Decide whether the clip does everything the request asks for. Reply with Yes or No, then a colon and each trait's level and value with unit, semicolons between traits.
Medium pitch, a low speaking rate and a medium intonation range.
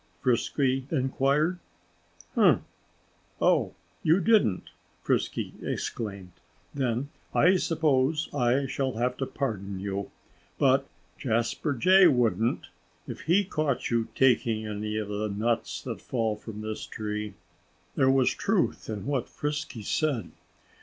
No: low, 125 Hz; slow, 120 wpm; average, 4.7 semitones